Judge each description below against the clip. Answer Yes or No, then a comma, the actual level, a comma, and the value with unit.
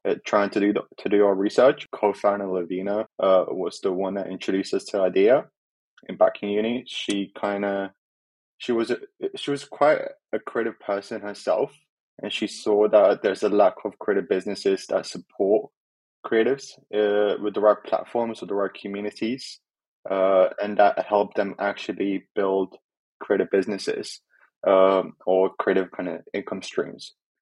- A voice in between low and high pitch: No, low, 100 Hz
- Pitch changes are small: Yes, narrow, 1.7 semitones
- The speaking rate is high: No, average, 160 wpm